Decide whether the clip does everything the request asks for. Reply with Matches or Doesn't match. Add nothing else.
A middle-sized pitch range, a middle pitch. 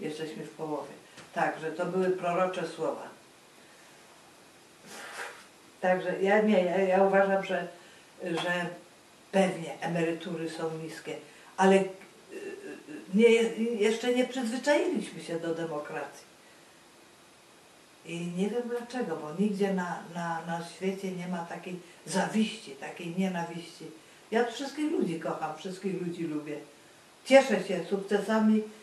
Matches